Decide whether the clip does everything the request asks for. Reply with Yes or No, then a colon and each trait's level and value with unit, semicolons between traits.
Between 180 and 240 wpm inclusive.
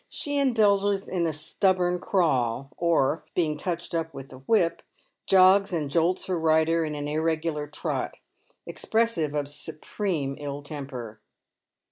No: slow, 135 wpm